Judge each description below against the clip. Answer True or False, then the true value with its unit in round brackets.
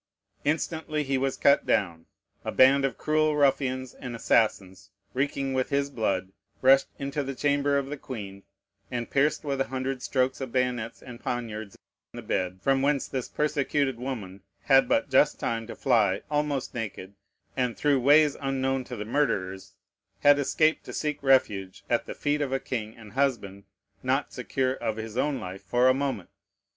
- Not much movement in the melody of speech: False (3.7 semitones)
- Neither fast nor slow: True (175 wpm)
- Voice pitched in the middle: False (130 Hz)